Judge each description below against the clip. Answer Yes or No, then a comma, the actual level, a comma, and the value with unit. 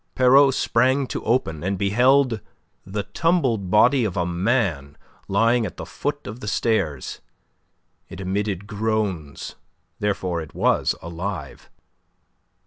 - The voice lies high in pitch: No, low, 105 Hz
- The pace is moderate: No, slow, 125 wpm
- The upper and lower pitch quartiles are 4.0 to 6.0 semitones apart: Yes, average, 5.2 semitones